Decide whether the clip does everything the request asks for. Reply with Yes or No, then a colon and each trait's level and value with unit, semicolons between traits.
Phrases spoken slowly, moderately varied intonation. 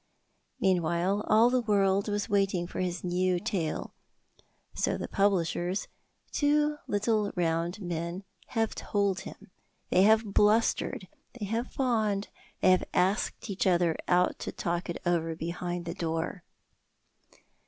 Yes: slow, 130 wpm; average, 3.2 semitones